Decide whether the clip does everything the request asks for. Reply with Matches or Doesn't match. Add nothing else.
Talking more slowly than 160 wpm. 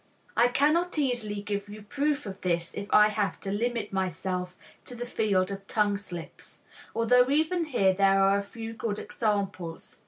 Doesn't match